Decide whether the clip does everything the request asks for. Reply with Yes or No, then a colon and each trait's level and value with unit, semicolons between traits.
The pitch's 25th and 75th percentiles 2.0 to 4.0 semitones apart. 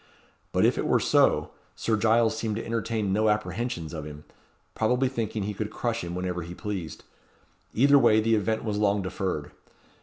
Yes: average, 3.6 semitones